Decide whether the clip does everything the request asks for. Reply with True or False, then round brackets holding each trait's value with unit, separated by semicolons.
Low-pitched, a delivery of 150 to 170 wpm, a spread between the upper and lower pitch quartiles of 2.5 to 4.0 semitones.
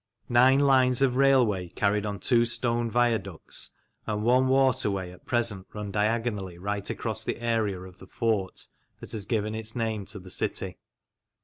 True (110 Hz; 165 wpm; 3.3 semitones)